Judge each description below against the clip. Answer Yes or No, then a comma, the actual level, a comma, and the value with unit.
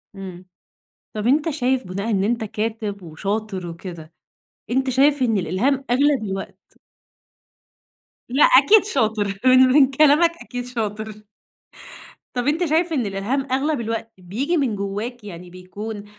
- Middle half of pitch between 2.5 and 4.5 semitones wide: No, average, 5.3 semitones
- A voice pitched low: No, high, 225 Hz